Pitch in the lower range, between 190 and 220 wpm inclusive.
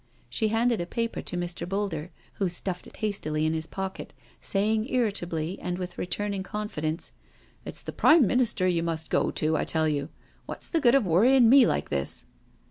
No: high, 190 Hz; average, 195 wpm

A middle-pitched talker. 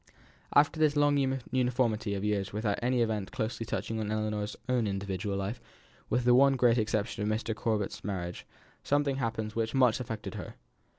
No: low, 110 Hz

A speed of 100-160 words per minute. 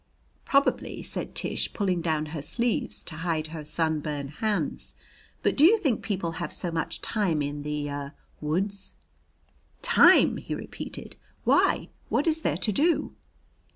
Yes: average, 150 wpm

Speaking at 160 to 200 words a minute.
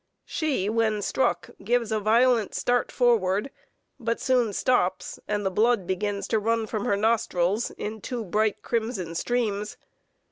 No: average, 145 wpm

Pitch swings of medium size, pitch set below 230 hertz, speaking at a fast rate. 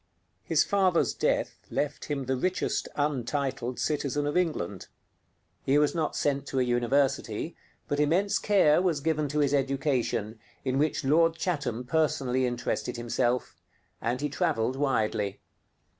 No: average, 3.4 semitones; medium, 140 Hz; average, 140 wpm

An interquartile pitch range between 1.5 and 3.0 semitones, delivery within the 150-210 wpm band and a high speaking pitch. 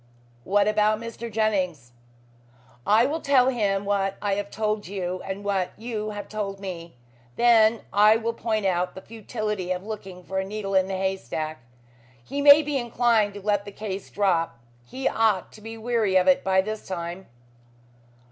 Yes: average, 2.7 semitones; average, 175 wpm; high, 205 Hz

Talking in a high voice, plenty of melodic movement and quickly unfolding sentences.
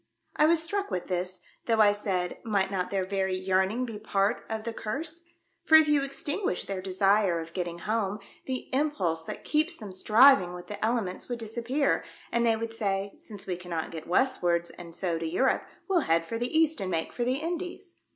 Yes: high, 210 Hz; wide, 6.1 semitones; fast, 210 wpm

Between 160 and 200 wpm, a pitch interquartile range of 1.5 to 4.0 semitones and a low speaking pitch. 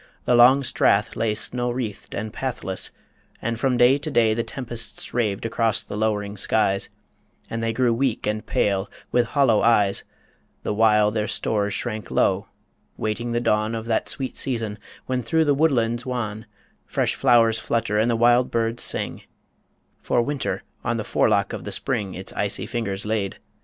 Yes: average, 170 wpm; narrow, 2.4 semitones; low, 115 Hz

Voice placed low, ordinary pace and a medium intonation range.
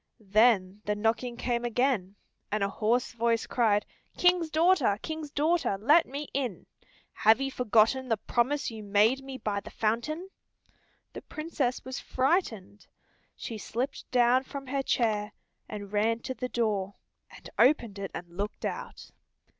No: high, 235 Hz; average, 150 wpm; average, 4.4 semitones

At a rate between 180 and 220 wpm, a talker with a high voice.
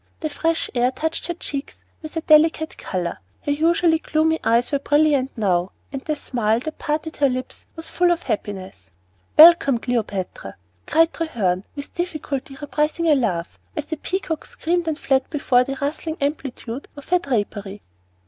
No: average, 165 wpm; very high, 285 Hz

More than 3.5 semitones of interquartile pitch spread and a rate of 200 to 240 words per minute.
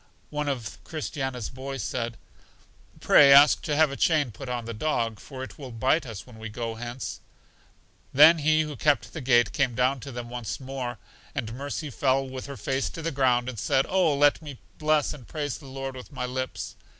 No: average, 3.0 semitones; fast, 205 wpm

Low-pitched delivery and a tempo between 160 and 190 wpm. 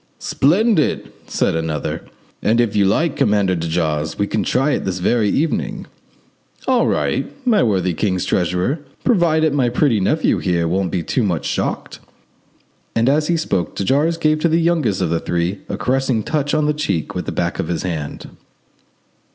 Yes: low, 110 Hz; average, 180 wpm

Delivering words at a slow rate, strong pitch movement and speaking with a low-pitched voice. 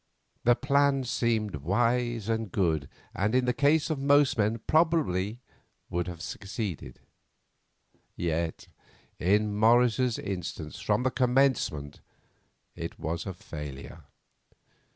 Yes: slow, 110 wpm; wide, 6.3 semitones; low, 110 Hz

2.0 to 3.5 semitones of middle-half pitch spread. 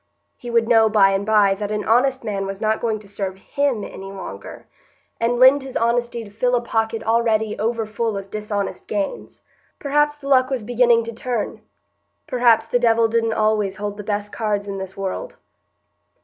Yes: average, 2.7 semitones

